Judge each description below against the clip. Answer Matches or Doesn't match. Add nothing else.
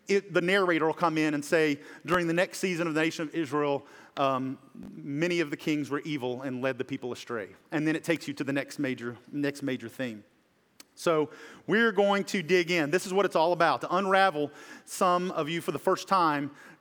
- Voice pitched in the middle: Matches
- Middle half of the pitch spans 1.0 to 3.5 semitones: Doesn't match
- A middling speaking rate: Doesn't match